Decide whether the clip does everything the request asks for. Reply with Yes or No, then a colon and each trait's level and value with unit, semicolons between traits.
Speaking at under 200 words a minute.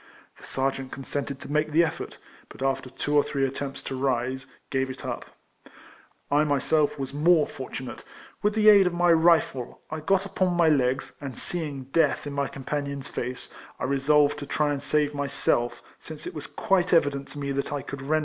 No: fast, 205 wpm